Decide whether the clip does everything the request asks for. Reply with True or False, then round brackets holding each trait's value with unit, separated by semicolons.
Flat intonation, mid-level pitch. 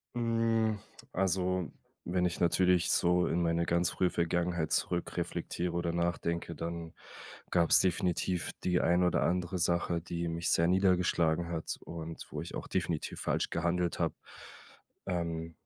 False (1.2 semitones; 85 Hz)